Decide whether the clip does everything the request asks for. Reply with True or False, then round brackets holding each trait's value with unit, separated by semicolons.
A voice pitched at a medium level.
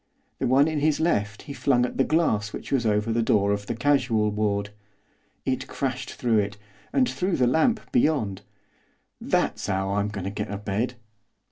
False (115 Hz)